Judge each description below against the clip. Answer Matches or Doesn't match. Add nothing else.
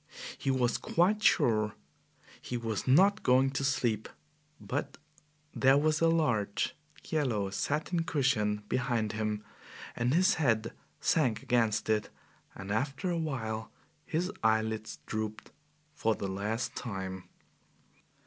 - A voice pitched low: Matches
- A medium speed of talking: Doesn't match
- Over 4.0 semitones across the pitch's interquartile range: Matches